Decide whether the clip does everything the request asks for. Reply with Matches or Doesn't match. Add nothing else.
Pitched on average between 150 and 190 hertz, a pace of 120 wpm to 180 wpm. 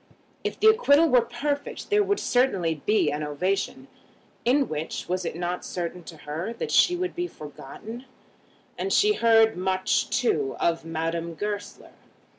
Doesn't match